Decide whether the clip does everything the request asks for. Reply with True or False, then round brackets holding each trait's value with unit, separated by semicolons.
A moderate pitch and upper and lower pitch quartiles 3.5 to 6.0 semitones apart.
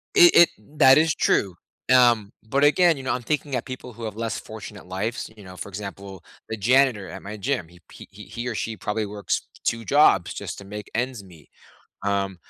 False (110 Hz; 4.5 semitones)